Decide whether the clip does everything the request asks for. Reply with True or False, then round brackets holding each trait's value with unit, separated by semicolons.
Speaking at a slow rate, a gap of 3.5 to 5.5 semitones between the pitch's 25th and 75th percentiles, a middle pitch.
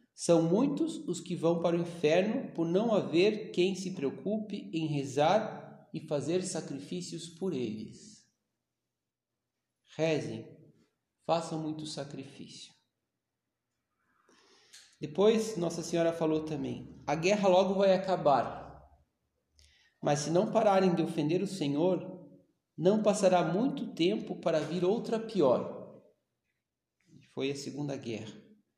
True (115 wpm; 3.9 semitones; 170 Hz)